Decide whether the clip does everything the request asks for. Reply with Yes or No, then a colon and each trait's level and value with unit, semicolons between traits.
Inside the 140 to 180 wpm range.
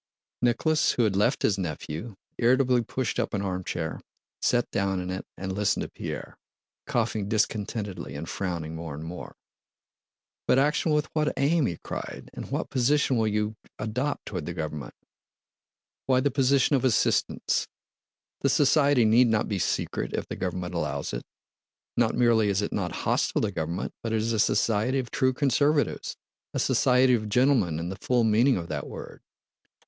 Yes: average, 170 wpm